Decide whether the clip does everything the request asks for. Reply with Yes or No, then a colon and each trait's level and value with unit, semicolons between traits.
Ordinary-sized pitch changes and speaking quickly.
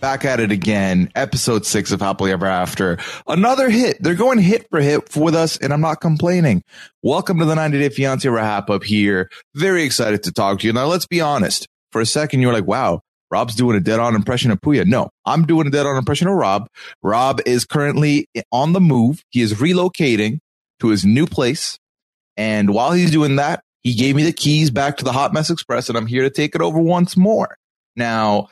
No: wide, 6.4 semitones; fast, 215 wpm